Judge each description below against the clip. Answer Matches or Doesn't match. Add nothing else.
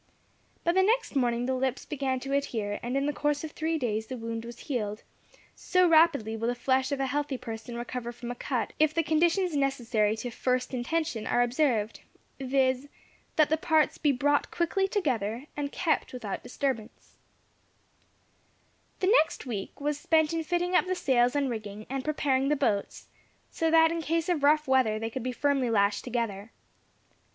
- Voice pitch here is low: Doesn't match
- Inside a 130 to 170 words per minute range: Doesn't match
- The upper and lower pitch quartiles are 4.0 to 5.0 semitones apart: Matches